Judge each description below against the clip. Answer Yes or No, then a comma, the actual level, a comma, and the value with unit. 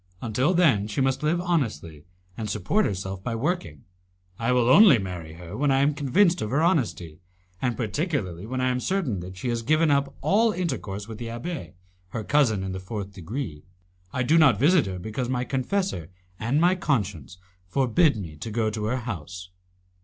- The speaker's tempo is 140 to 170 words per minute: No, average, 190 wpm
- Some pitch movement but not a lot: No, wide, 7.1 semitones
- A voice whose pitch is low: Yes, low, 120 Hz